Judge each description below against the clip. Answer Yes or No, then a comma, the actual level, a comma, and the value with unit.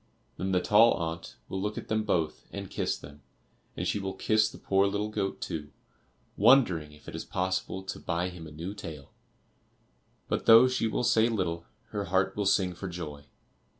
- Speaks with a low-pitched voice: Yes, very low, 95 Hz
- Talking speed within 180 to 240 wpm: Yes, average, 190 wpm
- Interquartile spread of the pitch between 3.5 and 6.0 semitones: Yes, average, 3.9 semitones